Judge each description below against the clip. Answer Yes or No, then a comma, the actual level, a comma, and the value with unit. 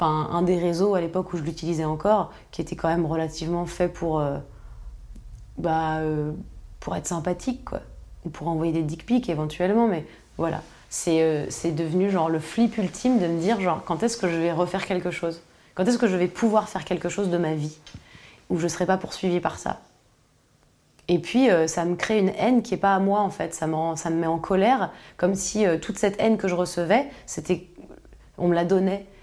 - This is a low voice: No, medium, 175 Hz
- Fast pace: Yes, fast, 225 wpm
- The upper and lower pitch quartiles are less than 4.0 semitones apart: Yes, average, 3.0 semitones